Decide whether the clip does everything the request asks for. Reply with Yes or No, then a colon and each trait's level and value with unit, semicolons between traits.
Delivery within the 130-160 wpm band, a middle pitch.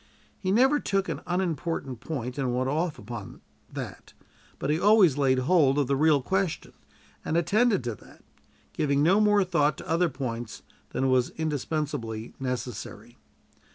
Yes: average, 155 wpm; medium, 145 Hz